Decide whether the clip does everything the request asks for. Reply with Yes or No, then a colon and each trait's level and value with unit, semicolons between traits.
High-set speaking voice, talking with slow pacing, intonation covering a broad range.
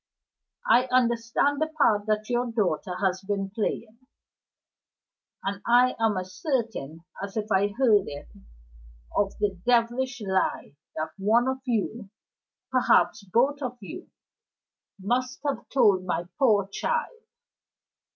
No: high, 220 Hz; slow, 130 wpm; average, 4.3 semitones